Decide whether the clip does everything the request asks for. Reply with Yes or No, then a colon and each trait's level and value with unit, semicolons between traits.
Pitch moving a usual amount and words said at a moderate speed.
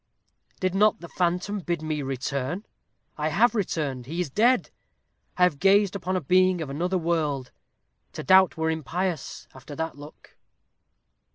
Yes: average, 3.9 semitones; average, 155 wpm